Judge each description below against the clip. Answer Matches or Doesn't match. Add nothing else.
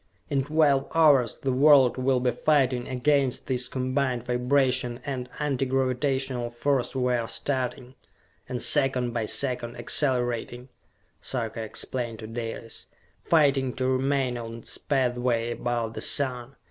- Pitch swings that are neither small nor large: Doesn't match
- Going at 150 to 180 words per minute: Doesn't match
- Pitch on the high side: Doesn't match